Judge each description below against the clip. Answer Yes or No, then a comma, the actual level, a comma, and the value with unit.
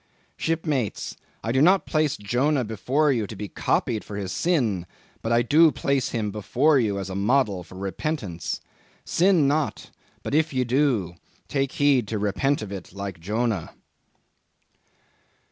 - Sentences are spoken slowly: No, average, 155 wpm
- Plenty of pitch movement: Yes, wide, 6.3 semitones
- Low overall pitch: Yes, low, 120 Hz